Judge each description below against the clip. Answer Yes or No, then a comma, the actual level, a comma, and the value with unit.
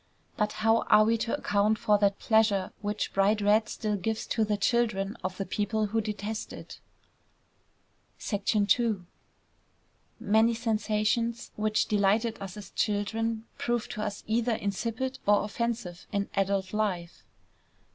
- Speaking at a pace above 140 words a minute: No, slow, 135 wpm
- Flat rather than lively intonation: Yes, narrow, 1.8 semitones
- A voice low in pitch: No, high, 215 Hz